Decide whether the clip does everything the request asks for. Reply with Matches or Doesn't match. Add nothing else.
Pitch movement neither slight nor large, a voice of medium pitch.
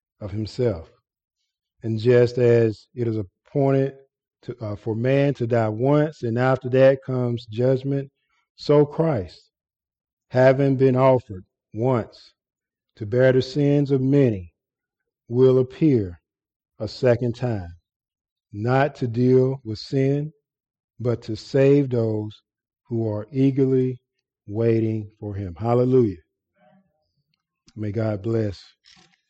Doesn't match